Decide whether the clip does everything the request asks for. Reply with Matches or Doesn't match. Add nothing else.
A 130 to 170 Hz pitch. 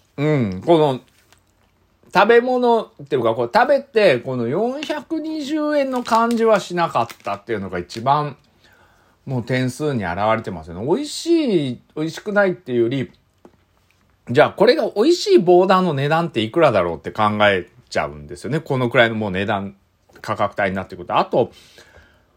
Matches